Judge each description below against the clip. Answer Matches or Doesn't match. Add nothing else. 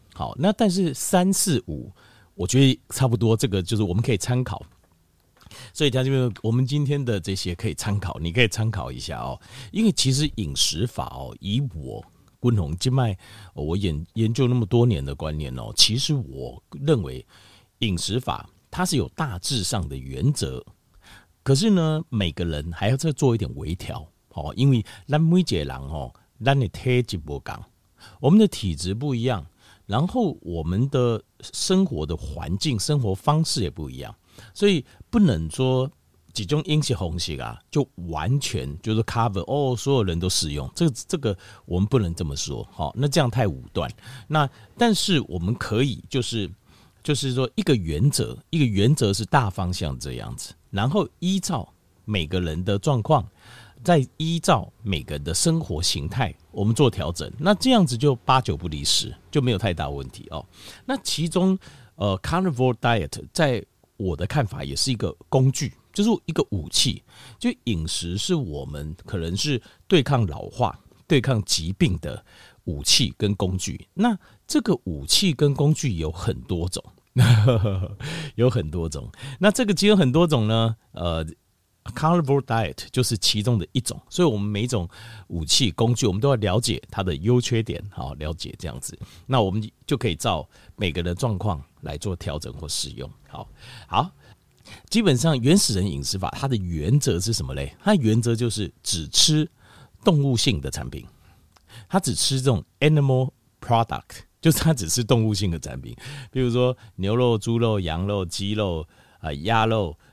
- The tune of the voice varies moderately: Doesn't match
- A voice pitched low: Matches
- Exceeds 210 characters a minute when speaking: Matches